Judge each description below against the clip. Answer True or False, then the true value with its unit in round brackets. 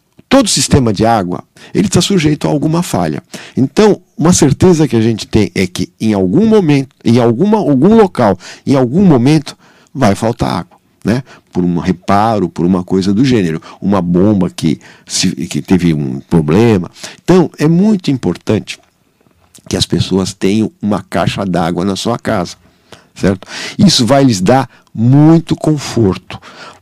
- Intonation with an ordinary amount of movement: False (8.9 semitones)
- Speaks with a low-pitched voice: True (125 Hz)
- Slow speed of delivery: False (155 wpm)